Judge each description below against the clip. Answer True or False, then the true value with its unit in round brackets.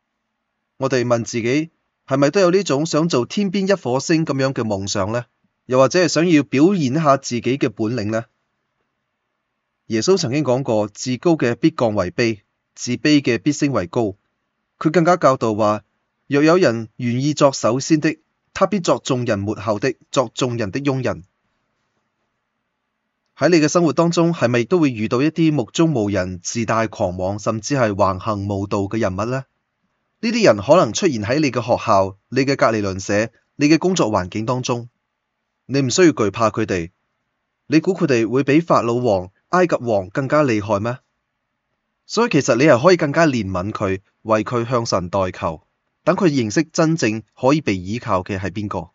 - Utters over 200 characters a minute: True (255 characters per minute)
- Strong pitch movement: True (5.7 semitones)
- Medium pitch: False (125 Hz)